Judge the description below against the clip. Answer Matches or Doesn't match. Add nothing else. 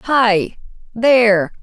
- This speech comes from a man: Doesn't match